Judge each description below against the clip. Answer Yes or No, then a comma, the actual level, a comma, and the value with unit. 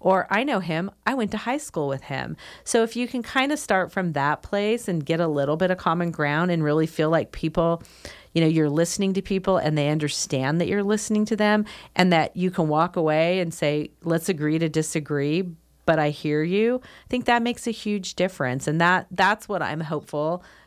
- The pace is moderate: No, fast, 225 wpm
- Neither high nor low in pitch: Yes, medium, 175 Hz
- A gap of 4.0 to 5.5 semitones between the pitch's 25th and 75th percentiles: Yes, average, 4.6 semitones